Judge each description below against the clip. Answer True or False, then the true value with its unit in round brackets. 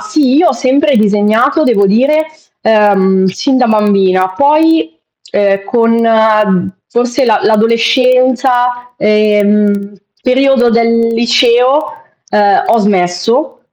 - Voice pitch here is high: True (230 Hz)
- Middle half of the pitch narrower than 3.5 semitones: False (3.8 semitones)